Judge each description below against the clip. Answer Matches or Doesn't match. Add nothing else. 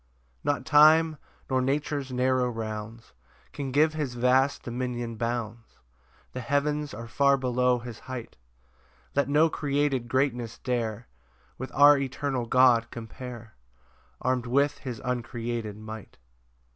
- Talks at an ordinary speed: Doesn't match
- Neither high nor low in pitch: Doesn't match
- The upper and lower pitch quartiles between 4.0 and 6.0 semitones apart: Doesn't match